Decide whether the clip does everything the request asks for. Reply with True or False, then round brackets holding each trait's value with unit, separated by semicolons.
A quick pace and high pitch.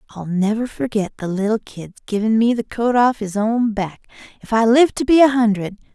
True (210 wpm; 220 Hz)